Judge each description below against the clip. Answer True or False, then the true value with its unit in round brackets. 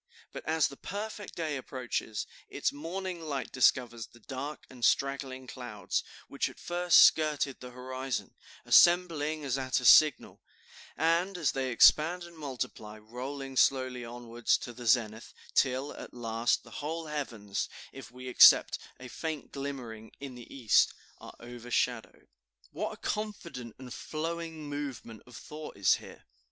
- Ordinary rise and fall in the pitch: True (4.2 semitones)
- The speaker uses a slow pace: False (145 wpm)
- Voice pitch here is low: True (130 Hz)